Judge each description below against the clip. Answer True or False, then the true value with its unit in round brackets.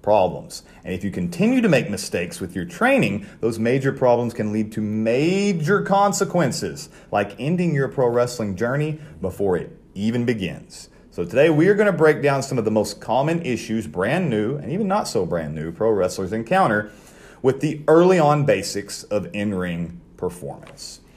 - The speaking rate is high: False (180 wpm)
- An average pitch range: False (6.9 semitones)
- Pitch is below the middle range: True (120 Hz)